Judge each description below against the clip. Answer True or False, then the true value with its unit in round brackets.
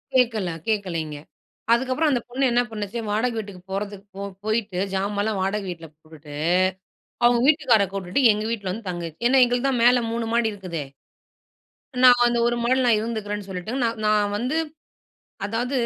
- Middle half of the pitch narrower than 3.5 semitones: False (3.8 semitones)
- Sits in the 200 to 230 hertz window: True (215 Hz)